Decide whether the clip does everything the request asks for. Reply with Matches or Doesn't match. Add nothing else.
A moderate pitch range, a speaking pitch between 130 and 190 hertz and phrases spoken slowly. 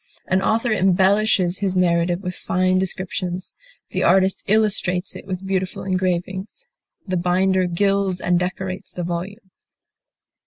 Doesn't match